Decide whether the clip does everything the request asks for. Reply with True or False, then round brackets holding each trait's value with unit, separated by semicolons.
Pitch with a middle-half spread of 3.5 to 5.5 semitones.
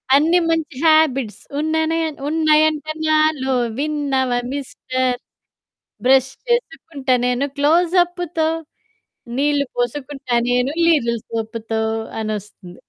True (4.0 semitones)